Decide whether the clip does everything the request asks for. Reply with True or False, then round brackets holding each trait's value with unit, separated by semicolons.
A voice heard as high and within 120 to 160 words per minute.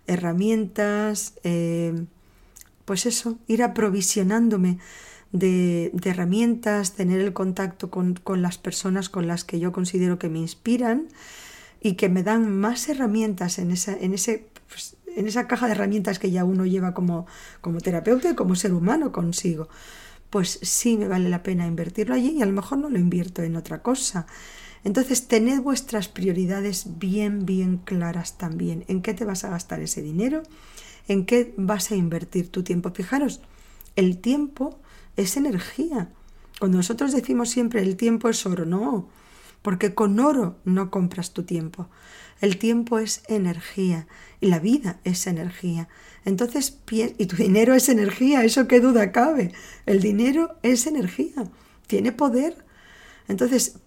True (200 Hz; 155 wpm)